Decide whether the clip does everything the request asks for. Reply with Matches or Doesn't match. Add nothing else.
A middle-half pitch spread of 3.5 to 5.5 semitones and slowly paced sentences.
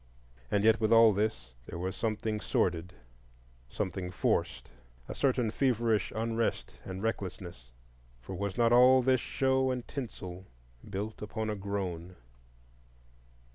Matches